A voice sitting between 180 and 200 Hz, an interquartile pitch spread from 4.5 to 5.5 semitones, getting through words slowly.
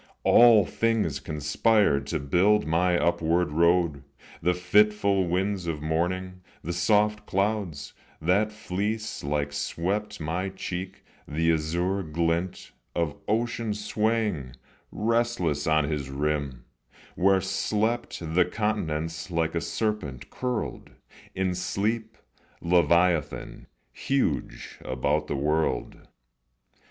No: very low, 90 Hz; average, 5.0 semitones; slow, 105 wpm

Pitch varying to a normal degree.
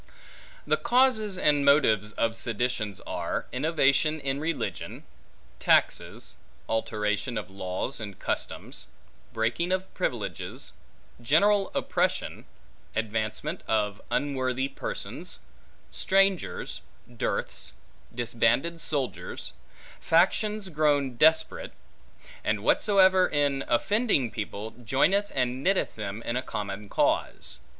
No: wide, 7.9 semitones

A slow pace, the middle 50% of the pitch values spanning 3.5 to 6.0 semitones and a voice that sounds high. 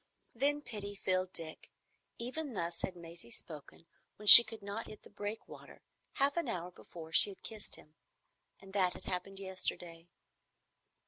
No: average, 155 wpm; average, 4.3 semitones; high, 195 Hz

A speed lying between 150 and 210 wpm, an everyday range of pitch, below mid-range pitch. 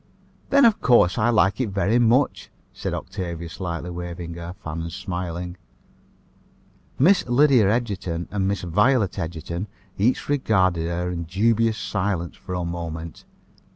No: average, 140 wpm; average, 4.7 semitones; very low, 95 Hz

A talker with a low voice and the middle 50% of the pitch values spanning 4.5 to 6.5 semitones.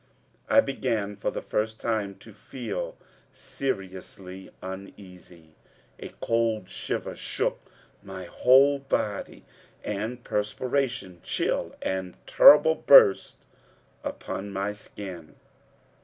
Yes: low, 105 Hz; average, 4.8 semitones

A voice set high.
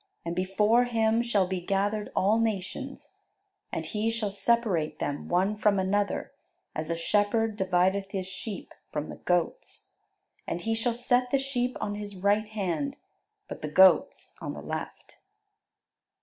Yes: high, 205 Hz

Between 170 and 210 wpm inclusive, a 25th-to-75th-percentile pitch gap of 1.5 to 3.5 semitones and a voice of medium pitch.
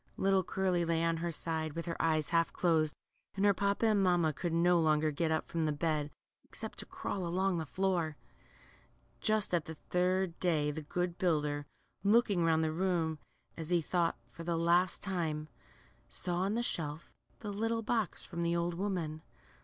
Yes: average, 185 wpm; average, 2.8 semitones; medium, 170 Hz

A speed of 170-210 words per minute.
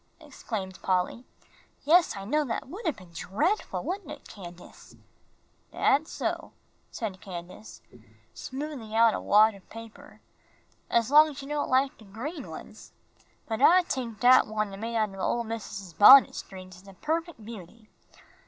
No: average, 160 wpm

